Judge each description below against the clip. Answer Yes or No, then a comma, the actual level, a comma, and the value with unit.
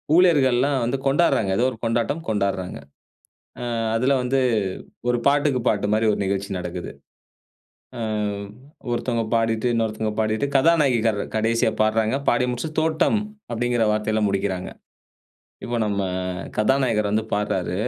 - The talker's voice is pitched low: Yes, low, 115 Hz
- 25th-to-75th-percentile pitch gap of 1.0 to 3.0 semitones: No, average, 3.6 semitones